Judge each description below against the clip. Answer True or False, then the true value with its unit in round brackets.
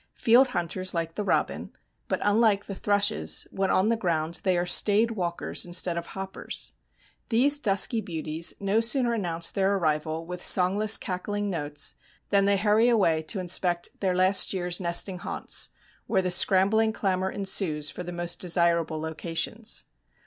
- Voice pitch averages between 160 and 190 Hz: True (185 Hz)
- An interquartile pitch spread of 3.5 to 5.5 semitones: False (3.1 semitones)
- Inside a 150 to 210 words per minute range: True (155 wpm)